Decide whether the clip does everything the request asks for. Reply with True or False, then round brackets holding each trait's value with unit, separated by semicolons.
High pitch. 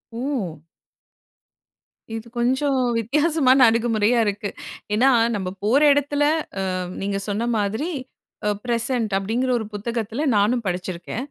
True (230 Hz)